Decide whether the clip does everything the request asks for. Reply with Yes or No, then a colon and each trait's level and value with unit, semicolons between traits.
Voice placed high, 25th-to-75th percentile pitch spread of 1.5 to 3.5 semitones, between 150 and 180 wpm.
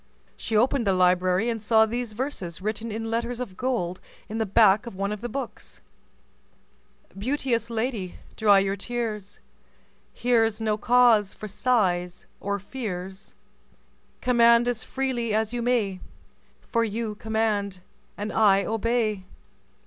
No: high, 220 Hz; average, 3.0 semitones; slow, 135 wpm